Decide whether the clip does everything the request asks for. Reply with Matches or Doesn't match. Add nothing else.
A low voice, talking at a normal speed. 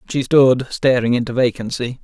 Matches